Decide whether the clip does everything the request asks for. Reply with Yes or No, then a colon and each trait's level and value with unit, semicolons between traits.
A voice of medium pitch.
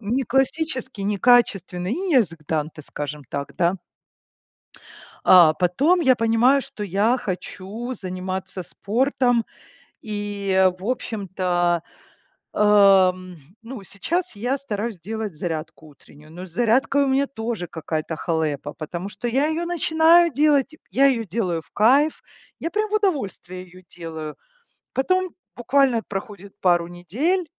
No: high, 205 Hz